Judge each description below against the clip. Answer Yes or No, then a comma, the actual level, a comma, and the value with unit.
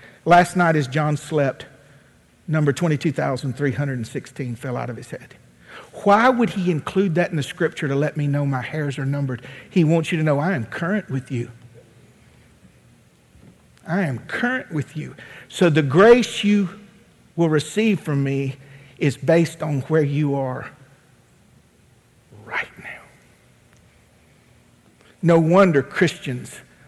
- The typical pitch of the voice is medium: Yes, medium, 150 Hz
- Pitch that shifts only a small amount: No, average, 4.2 semitones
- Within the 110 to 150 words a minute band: Yes, average, 140 wpm